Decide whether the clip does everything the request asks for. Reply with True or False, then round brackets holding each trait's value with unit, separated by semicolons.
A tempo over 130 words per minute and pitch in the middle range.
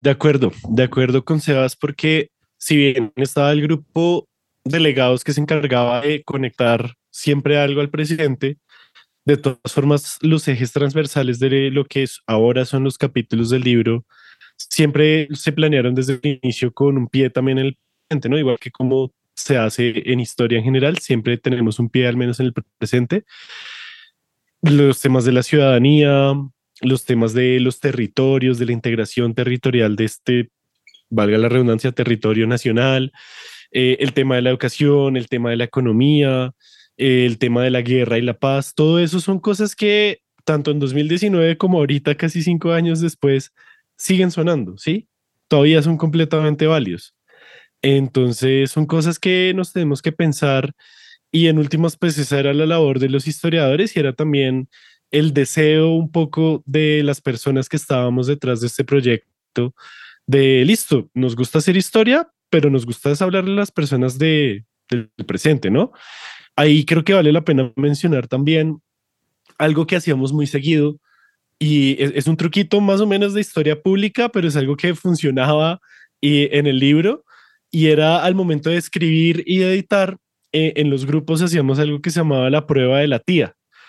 True (170 wpm; 145 Hz)